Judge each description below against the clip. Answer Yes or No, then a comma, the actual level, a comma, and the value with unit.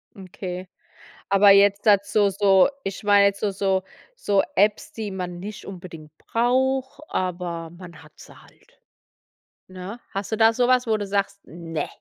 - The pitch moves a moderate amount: No, narrow, 2.3 semitones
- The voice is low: No, high, 195 Hz